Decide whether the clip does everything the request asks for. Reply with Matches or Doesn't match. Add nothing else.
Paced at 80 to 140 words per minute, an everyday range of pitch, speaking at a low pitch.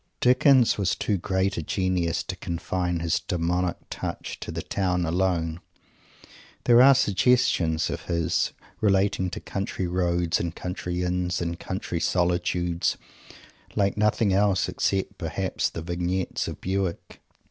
Doesn't match